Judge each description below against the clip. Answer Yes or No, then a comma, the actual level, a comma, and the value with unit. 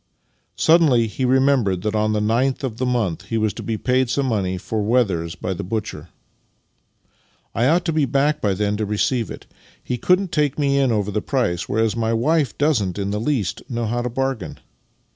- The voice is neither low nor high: No, low, 115 Hz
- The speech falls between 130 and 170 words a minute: No, fast, 205 wpm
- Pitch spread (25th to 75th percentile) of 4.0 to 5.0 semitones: Yes, average, 4.3 semitones